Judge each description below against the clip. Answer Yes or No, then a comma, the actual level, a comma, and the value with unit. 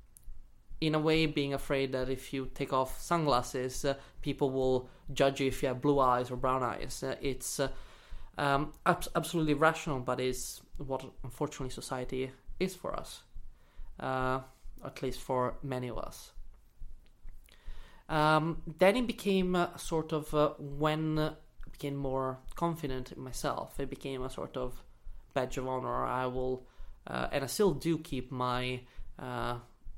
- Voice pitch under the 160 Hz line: Yes, low, 135 Hz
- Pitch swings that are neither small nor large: Yes, average, 3.1 semitones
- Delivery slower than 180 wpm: Yes, average, 160 wpm